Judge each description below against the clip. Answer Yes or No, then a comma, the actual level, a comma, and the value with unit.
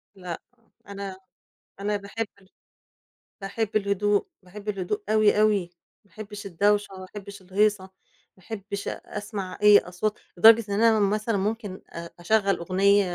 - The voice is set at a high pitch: Yes, high, 200 Hz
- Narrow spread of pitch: Yes, narrow, 1.8 semitones